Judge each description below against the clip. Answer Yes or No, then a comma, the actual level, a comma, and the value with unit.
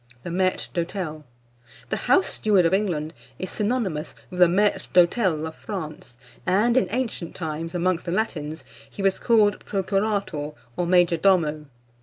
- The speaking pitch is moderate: Yes, medium, 180 Hz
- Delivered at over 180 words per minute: No, average, 150 wpm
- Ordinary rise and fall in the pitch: Yes, average, 3.9 semitones